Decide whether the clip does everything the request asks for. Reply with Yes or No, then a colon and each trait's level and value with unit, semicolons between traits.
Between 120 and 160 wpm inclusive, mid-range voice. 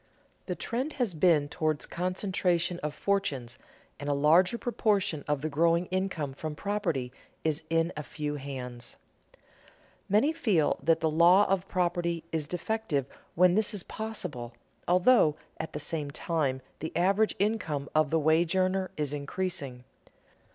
Yes: average, 145 wpm; medium, 165 Hz